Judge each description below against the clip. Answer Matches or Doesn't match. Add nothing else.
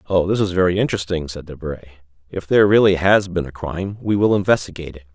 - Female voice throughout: Doesn't match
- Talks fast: Matches